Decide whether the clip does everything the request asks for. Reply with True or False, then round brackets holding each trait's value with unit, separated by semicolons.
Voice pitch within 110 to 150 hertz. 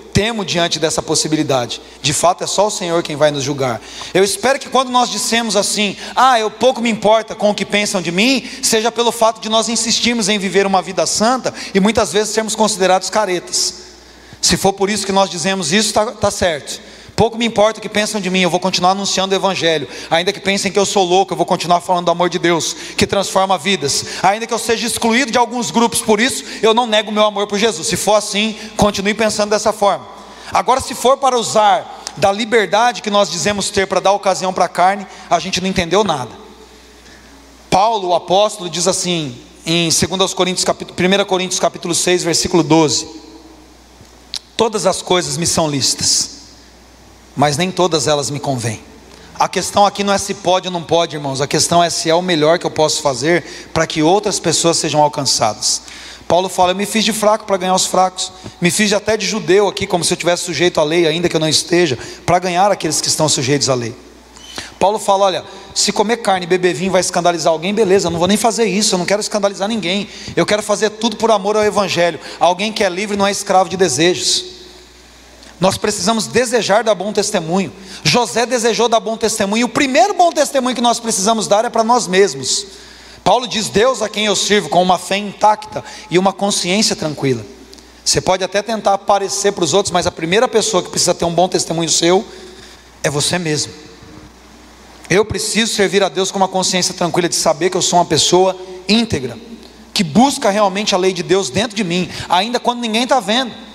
False (195 Hz)